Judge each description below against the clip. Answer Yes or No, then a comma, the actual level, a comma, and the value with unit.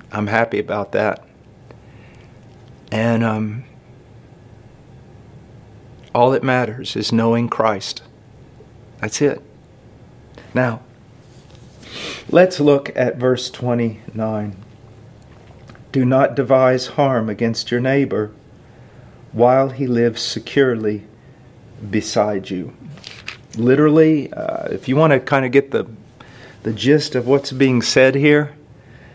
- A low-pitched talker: Yes, low, 125 Hz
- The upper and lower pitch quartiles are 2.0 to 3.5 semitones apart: Yes, narrow, 2.6 semitones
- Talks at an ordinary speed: No, slow, 105 wpm